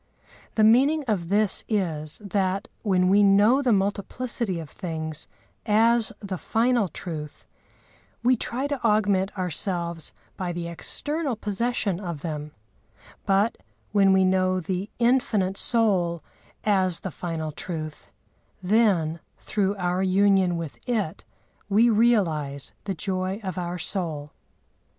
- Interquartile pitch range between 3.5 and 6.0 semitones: Yes, average, 3.8 semitones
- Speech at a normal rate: No, slow, 125 wpm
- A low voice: No, high, 190 Hz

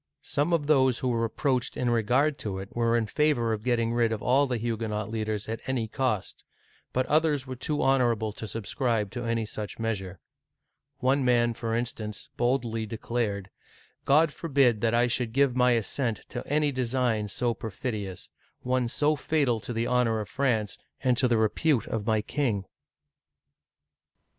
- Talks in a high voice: No, low, 120 Hz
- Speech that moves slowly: No, average, 170 wpm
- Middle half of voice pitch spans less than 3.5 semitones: Yes, average, 2.8 semitones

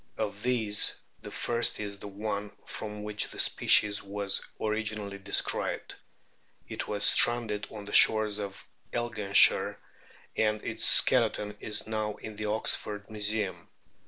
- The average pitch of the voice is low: Yes, low, 105 Hz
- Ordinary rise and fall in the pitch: No, narrow, 1.1 semitones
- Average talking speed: No, slow, 130 wpm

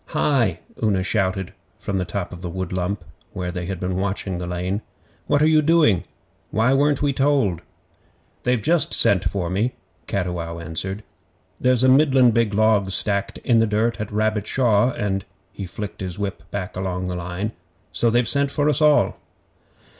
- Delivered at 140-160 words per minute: No, average, 175 wpm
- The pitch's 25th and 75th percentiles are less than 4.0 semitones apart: No, average, 5.1 semitones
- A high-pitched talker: No, low, 100 Hz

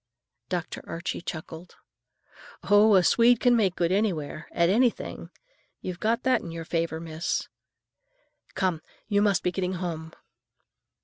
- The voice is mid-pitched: Yes, medium, 180 Hz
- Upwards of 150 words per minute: No, slow, 135 wpm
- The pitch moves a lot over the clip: No, average, 3.7 semitones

